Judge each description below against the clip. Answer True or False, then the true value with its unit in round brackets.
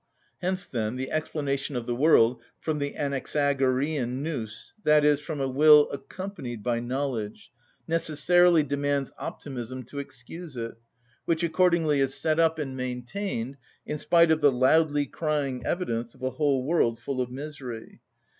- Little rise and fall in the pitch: False (3.5 semitones)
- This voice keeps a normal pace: True (145 wpm)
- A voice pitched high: False (140 Hz)